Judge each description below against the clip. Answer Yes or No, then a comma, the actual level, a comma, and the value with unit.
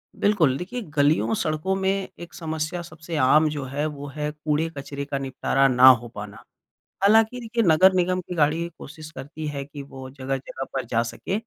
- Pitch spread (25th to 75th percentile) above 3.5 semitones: Yes, average, 4.1 semitones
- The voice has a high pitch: No, medium, 150 Hz